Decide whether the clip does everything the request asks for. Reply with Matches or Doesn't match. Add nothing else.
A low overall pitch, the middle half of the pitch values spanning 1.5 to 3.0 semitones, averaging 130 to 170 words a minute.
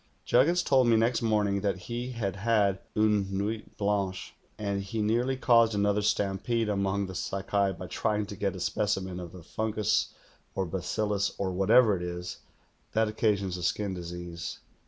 Matches